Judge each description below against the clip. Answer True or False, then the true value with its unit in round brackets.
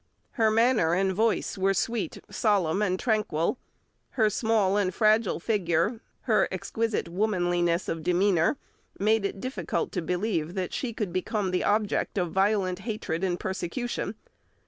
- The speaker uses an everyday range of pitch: True (3.5 semitones)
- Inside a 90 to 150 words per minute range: True (145 wpm)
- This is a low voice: False (195 Hz)